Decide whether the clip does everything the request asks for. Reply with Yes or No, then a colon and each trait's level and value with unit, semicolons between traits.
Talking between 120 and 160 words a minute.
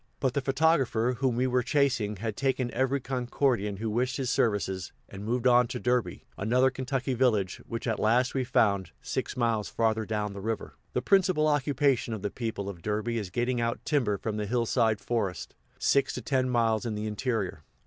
No: average, 190 wpm